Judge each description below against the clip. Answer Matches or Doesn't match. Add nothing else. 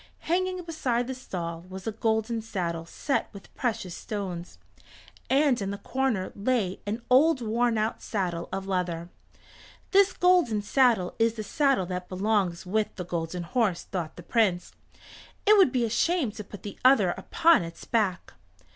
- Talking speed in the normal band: Matches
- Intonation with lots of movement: Matches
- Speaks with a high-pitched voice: Matches